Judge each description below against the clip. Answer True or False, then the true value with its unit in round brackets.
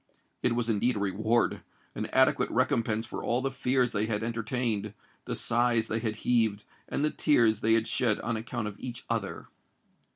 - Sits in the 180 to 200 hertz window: False (115 Hz)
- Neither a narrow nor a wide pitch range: False (2.0 semitones)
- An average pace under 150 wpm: False (175 wpm)